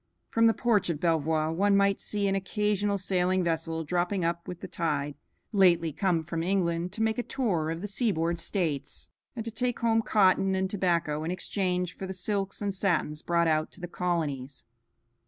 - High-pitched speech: No, medium, 180 Hz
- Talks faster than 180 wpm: Yes, average, 190 wpm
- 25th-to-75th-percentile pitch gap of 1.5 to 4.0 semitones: Yes, average, 3.3 semitones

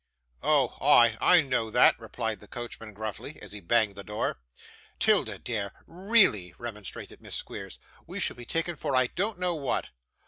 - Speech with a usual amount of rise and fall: No, wide, 6.3 semitones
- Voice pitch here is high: No, low, 120 Hz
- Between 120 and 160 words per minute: No, average, 170 wpm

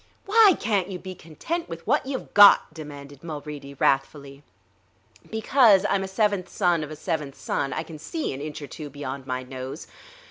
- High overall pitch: No, medium, 155 Hz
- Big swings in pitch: Yes, wide, 5.9 semitones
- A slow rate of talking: No, average, 180 wpm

